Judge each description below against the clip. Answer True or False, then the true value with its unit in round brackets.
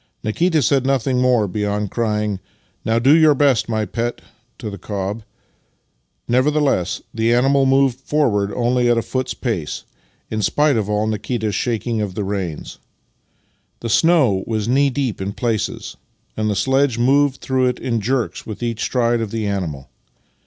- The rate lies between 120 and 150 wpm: False (165 wpm)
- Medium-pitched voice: False (115 Hz)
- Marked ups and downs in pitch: False (3.9 semitones)